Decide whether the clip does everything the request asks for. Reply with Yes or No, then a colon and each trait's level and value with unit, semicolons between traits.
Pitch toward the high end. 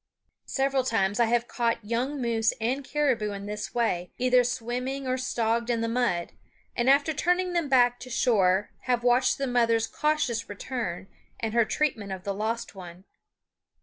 Yes: high, 240 Hz